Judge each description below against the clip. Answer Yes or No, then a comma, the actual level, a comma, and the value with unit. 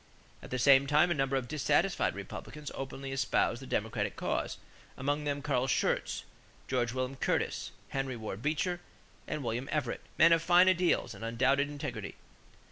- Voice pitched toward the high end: No, low, 135 Hz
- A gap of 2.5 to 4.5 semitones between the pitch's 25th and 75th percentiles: Yes, average, 3.0 semitones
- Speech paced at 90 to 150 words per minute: No, average, 160 wpm